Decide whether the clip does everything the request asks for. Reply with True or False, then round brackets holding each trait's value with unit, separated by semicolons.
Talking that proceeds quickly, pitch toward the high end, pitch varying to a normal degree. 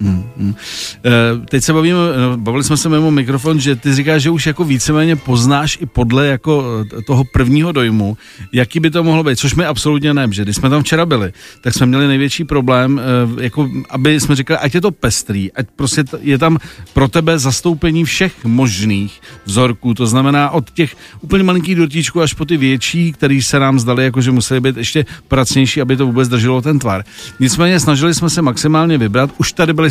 False (195 wpm; 140 Hz; 4.2 semitones)